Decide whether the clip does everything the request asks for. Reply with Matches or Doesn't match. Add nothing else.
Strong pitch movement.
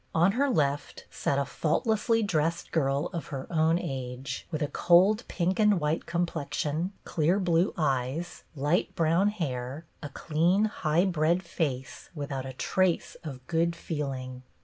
Doesn't match